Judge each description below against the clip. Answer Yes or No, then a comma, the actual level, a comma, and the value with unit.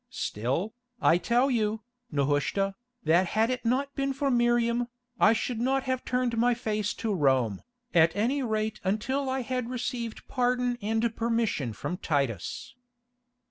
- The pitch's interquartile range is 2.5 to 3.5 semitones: No, average, 4.7 semitones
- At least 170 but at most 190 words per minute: No, average, 145 wpm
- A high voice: Yes, high, 230 Hz